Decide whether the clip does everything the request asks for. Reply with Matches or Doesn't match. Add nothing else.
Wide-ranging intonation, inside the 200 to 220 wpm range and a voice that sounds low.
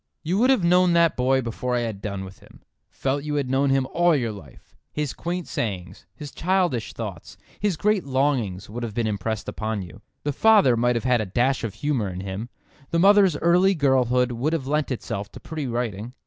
Matches